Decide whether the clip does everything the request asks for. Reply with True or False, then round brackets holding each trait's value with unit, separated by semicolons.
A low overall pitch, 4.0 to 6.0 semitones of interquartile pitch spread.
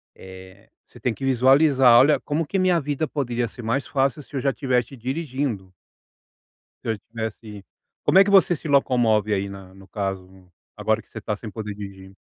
True (120 Hz; 5.5 semitones)